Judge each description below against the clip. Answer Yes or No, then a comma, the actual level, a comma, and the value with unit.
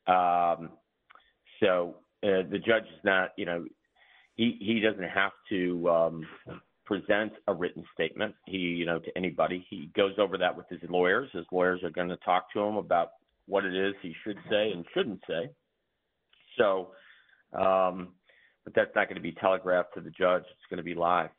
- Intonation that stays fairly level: Yes, narrow, 1.8 semitones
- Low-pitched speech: Yes, very low, 90 Hz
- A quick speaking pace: No, average, 185 wpm